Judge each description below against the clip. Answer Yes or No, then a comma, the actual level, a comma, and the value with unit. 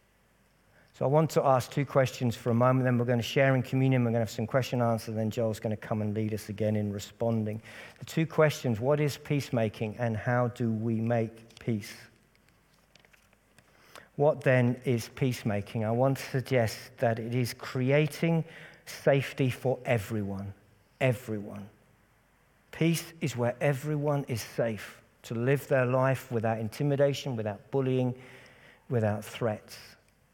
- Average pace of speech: Yes, average, 160 wpm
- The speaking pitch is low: Yes, low, 125 Hz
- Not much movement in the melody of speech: No, average, 3.2 semitones